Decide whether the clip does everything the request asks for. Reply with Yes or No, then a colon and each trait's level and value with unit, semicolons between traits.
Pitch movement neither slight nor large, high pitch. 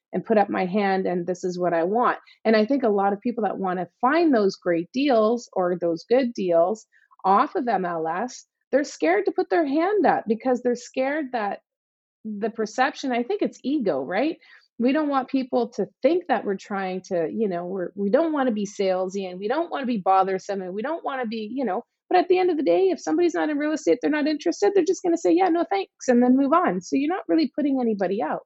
No: wide, 7.8 semitones; high, 245 Hz